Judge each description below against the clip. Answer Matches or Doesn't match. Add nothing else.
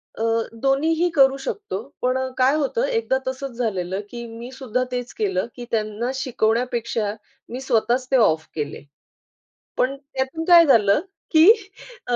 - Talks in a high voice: Matches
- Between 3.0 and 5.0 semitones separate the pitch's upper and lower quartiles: Matches